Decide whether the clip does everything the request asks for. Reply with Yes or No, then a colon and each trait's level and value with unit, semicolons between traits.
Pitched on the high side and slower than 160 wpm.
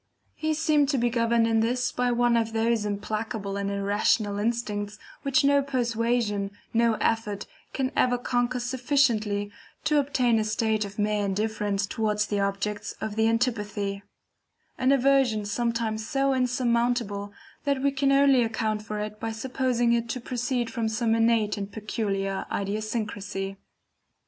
Yes: high, 225 Hz; average, 150 wpm